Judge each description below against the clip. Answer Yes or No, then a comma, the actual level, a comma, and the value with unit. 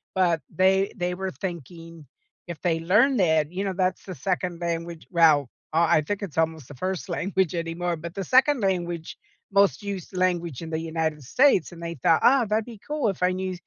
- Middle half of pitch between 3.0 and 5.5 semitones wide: No, narrow, 2.6 semitones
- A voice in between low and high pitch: Yes, medium, 175 Hz